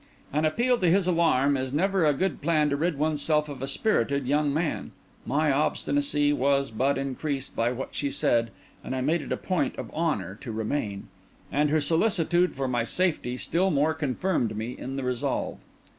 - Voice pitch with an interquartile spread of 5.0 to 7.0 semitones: No, average, 3.5 semitones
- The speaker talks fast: No, average, 190 wpm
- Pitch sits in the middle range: Yes, medium, 145 Hz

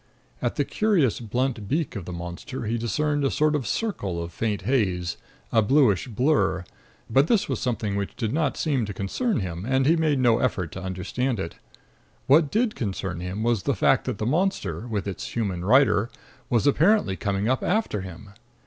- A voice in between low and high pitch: No, low, 115 Hz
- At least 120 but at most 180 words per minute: No, average, 190 wpm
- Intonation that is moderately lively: No, wide, 6.6 semitones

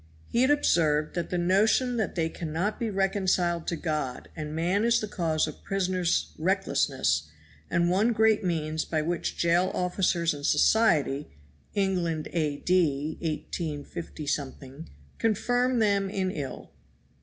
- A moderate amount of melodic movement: Yes, average, 4.2 semitones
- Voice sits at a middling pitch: Yes, medium, 175 Hz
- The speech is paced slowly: Yes, slow, 130 wpm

